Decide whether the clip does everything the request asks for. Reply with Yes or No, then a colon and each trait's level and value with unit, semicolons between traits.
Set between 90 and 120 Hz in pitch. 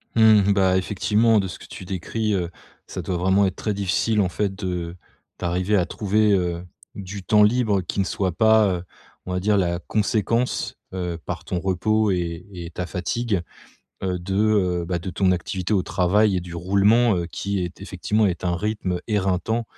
Yes: very low, 95 Hz